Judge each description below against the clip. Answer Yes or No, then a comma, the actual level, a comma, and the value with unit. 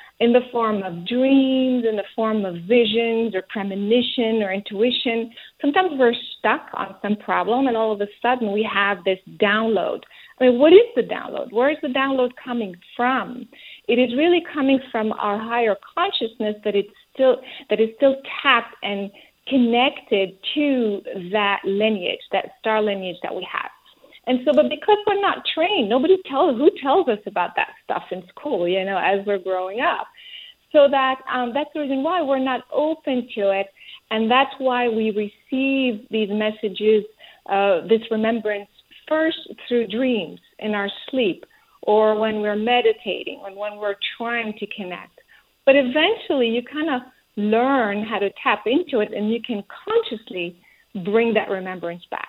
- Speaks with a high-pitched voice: Yes, high, 235 Hz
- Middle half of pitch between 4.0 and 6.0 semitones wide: Yes, average, 4.7 semitones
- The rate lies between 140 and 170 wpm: Yes, average, 165 wpm